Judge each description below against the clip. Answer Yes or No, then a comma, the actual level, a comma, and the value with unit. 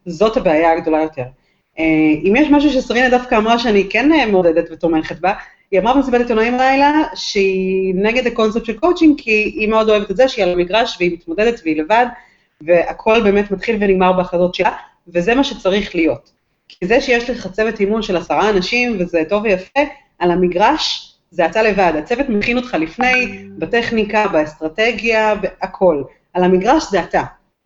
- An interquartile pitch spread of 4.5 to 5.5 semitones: Yes, average, 5.1 semitones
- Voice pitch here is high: Yes, high, 210 Hz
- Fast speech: Yes, fast, 165 wpm